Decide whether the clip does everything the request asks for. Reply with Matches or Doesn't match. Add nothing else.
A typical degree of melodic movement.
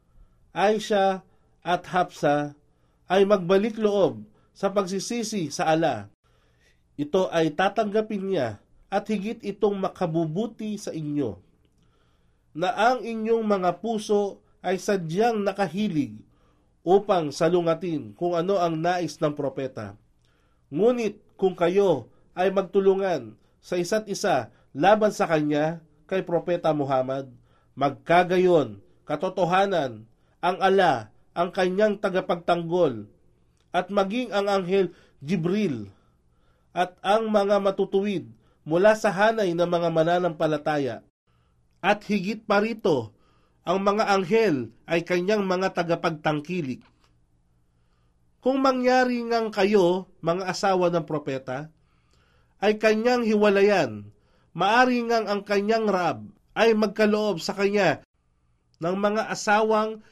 Doesn't match